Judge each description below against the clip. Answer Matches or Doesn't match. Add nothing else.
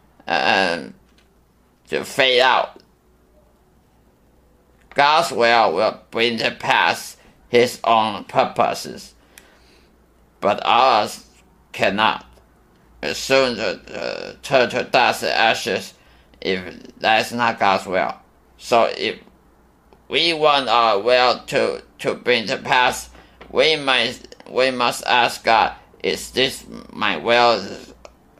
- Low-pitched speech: Matches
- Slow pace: Matches